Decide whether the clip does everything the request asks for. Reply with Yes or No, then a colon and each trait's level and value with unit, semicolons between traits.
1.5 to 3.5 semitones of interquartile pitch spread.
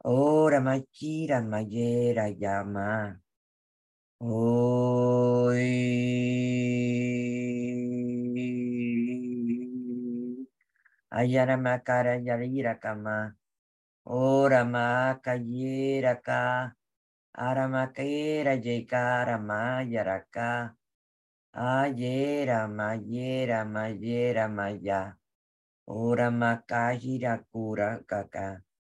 Yes: narrow, 2.4 semitones